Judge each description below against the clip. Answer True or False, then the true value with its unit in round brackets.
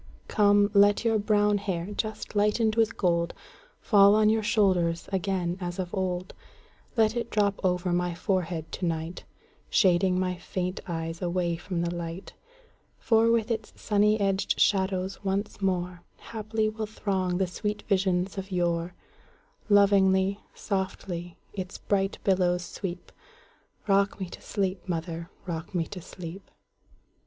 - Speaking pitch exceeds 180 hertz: True (190 Hz)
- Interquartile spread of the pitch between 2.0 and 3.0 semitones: True (2.7 semitones)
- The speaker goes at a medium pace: False (125 wpm)